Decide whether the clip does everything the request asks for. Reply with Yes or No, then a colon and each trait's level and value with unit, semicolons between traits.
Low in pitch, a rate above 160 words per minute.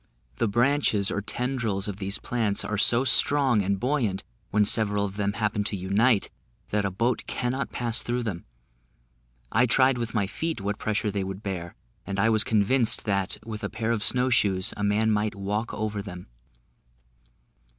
Yes: low, 105 Hz; average, 180 wpm